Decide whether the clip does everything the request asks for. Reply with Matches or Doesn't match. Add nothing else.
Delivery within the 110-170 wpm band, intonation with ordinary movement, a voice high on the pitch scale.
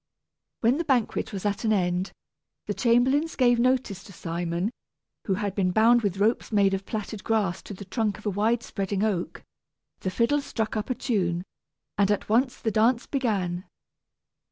Doesn't match